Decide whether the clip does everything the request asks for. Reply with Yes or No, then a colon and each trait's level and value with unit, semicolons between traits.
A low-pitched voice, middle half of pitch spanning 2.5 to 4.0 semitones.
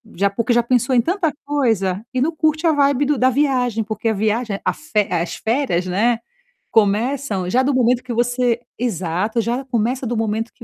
No: high, 240 Hz; average, 3.5 semitones